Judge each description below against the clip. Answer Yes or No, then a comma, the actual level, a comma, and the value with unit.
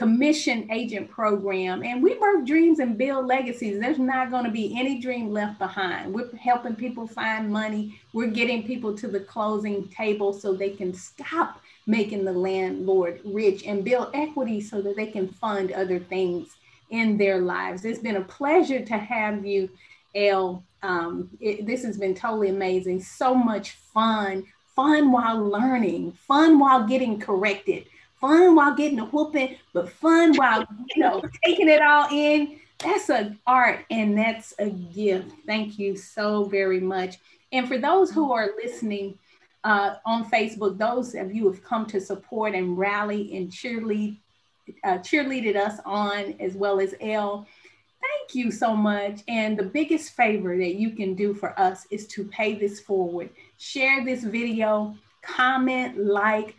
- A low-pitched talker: No, high, 215 Hz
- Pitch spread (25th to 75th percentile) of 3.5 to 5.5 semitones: Yes, average, 4.1 semitones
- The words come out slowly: No, average, 165 wpm